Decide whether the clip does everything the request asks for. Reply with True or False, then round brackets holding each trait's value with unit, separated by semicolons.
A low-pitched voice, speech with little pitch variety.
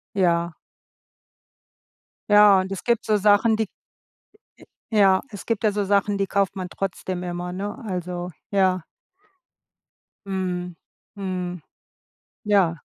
False (190 Hz; 2.2 semitones)